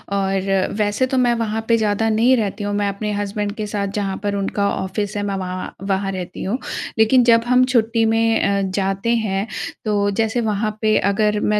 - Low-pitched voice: No, high, 210 Hz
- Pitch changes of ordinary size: No, narrow, 2.1 semitones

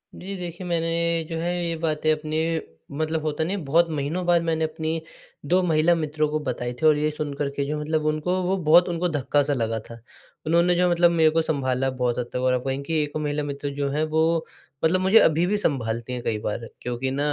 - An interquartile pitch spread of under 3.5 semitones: Yes, average, 3.0 semitones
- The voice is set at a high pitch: No, medium, 155 Hz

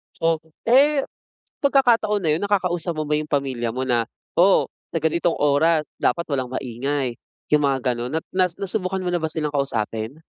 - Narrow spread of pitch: No, wide, 5.4 semitones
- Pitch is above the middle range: No, medium, 155 Hz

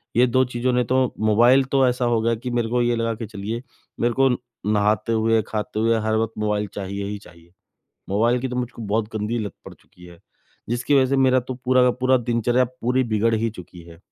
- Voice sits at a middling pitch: No, low, 115 Hz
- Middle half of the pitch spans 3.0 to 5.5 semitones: No, narrow, 2.6 semitones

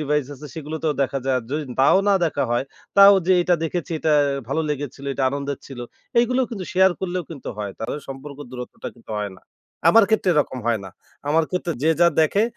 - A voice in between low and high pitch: Yes, medium, 150 Hz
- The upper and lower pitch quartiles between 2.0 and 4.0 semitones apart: No, average, 4.8 semitones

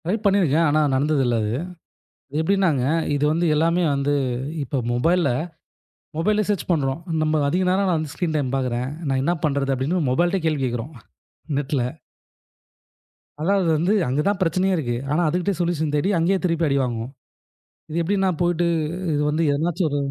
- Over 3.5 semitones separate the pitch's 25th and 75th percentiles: Yes, average, 4.1 semitones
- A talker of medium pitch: Yes, medium, 155 Hz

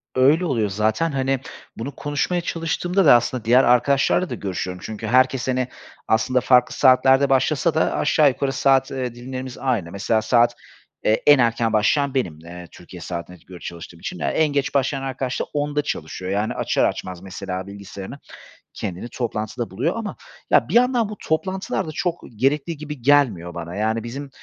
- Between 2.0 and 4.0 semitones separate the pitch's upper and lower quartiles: No, average, 5.3 semitones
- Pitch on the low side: Yes, low, 130 Hz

